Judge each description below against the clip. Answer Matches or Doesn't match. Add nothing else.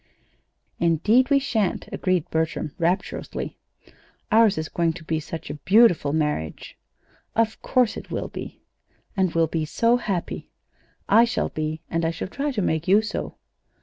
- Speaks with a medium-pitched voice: Matches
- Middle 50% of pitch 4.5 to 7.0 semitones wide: Matches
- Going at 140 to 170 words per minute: Matches